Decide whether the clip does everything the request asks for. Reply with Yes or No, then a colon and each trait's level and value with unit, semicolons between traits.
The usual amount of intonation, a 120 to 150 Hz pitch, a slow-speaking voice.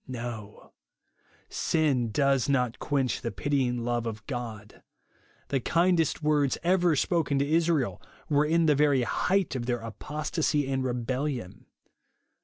Yes: average, 3.9 semitones; low, 135 Hz; slow, 130 wpm